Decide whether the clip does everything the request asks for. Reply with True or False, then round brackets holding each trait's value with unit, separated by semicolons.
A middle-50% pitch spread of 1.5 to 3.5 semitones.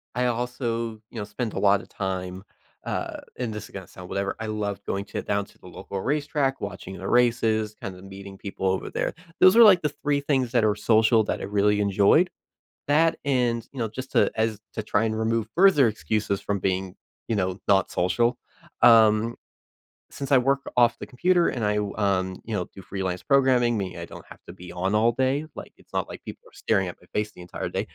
False (3.9 semitones)